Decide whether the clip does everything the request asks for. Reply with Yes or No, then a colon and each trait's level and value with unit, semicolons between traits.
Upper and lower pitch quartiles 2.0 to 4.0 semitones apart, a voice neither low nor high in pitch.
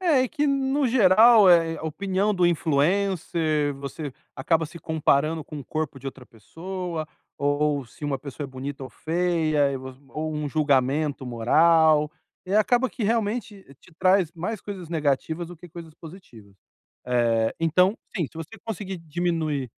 No: average, 4.5 semitones; medium, 160 Hz